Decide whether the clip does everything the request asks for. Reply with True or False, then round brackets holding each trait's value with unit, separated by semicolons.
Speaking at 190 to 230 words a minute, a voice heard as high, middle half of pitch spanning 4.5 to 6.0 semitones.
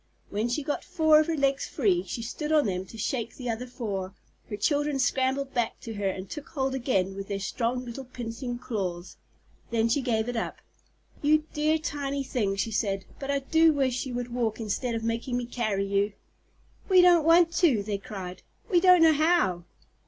True (200 wpm; 245 Hz; 5.2 semitones)